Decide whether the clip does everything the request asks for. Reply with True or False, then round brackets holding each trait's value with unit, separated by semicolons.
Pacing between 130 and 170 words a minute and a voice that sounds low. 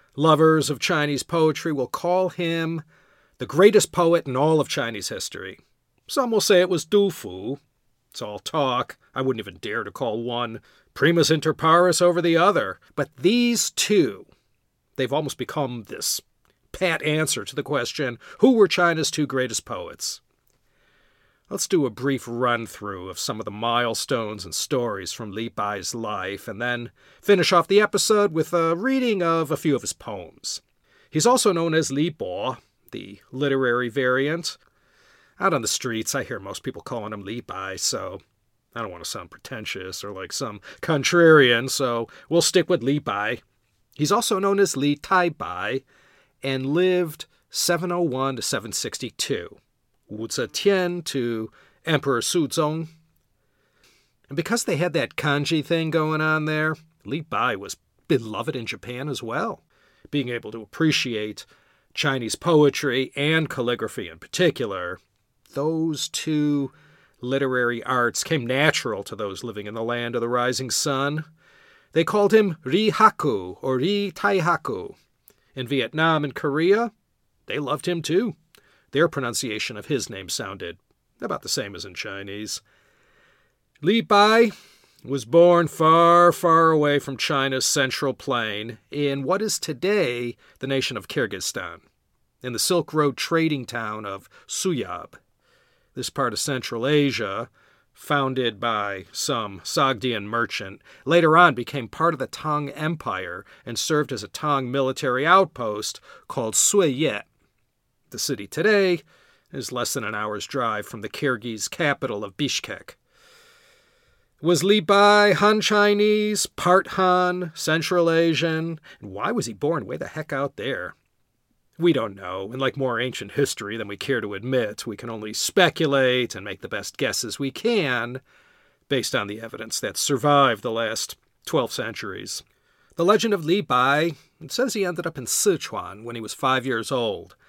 False (155 wpm; 145 Hz)